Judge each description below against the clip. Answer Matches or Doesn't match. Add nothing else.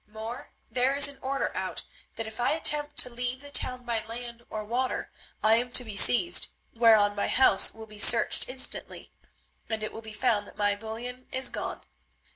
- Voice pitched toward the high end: Matches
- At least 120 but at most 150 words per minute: Doesn't match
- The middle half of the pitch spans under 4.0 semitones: Matches